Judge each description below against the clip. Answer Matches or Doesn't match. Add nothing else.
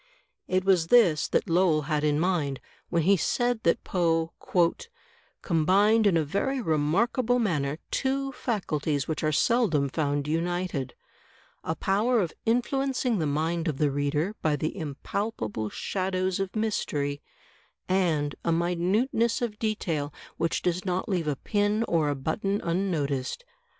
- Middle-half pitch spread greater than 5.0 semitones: Matches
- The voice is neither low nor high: Matches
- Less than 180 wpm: Matches